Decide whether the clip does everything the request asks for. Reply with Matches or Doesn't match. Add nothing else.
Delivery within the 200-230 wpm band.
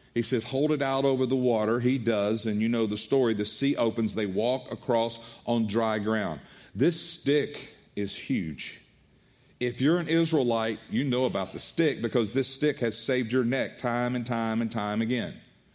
Doesn't match